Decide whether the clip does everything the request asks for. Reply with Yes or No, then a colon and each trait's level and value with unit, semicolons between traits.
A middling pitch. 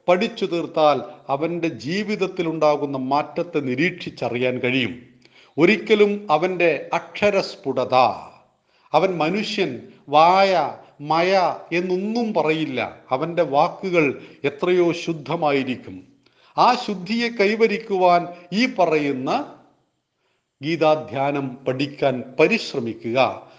Yes: medium, 165 Hz